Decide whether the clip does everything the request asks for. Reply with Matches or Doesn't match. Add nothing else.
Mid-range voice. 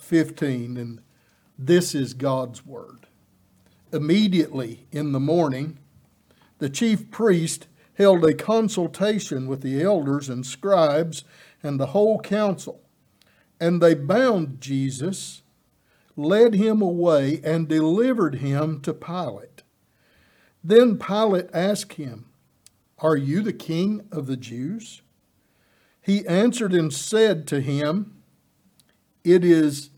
Matches